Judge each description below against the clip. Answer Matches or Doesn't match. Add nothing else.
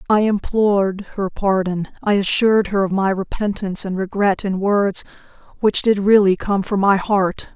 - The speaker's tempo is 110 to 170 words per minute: Matches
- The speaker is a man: Doesn't match